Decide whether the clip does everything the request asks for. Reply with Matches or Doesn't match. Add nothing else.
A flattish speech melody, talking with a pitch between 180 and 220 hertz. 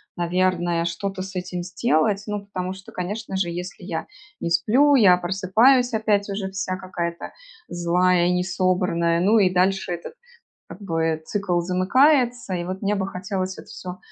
Matches